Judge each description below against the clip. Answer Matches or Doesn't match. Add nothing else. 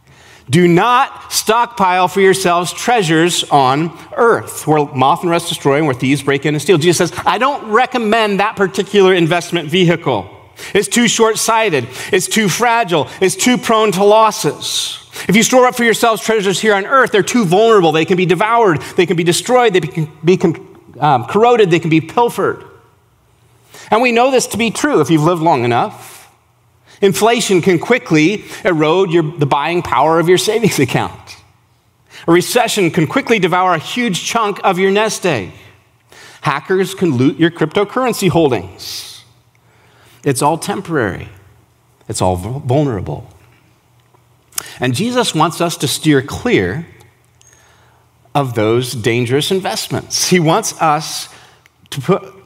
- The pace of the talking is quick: Doesn't match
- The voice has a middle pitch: Matches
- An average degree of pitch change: Doesn't match